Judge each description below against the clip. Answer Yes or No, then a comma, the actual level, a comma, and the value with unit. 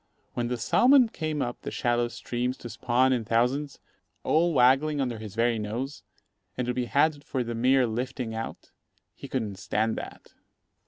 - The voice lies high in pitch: No, low, 125 Hz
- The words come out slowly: No, average, 170 wpm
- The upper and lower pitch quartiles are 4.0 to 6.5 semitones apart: No, average, 2.8 semitones